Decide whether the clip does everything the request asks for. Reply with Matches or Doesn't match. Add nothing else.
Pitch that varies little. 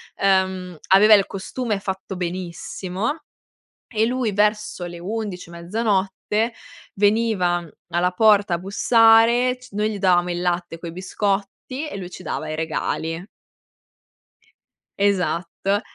Doesn't match